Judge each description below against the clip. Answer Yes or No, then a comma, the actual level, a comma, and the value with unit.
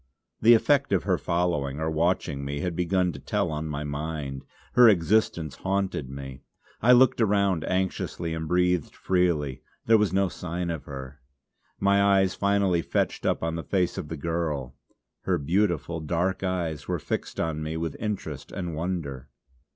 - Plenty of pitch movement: No, average, 3.9 semitones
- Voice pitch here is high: No, very low, 85 Hz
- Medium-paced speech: Yes, average, 165 wpm